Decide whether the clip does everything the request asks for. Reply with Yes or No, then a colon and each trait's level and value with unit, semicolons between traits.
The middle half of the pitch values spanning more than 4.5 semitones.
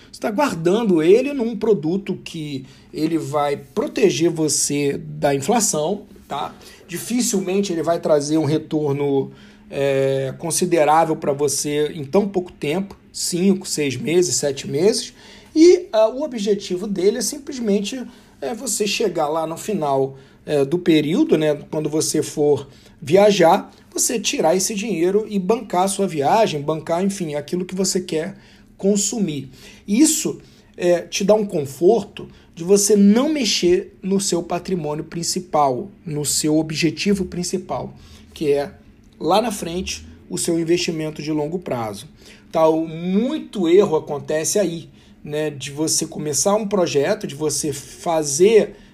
Yes: average, 5.1 semitones